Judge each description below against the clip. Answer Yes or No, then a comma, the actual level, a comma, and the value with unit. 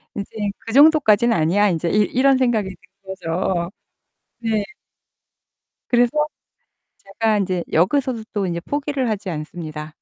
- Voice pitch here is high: Yes, high, 205 Hz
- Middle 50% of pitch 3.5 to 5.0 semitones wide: No, wide, 5.6 semitones